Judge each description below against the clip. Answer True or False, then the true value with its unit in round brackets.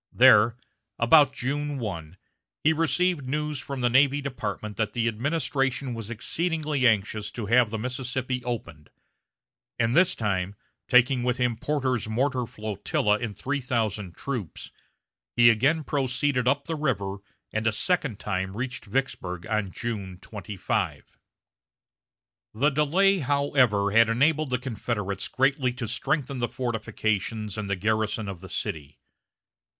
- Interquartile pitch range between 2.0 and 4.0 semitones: False (4.6 semitones)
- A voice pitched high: False (120 Hz)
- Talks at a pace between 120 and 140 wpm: True (135 wpm)